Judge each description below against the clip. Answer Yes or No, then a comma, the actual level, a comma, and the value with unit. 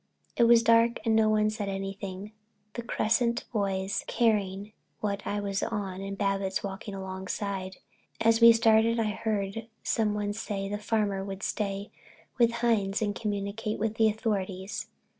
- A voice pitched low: No, high, 205 Hz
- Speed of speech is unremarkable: Yes, average, 150 wpm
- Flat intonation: Yes, narrow, 2.2 semitones